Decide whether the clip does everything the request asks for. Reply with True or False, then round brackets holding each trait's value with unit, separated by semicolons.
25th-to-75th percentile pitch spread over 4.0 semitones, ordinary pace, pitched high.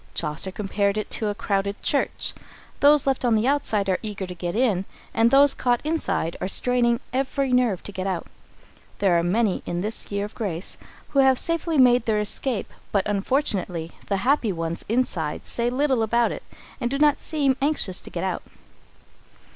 True (5.2 semitones; 185 wpm; 220 Hz)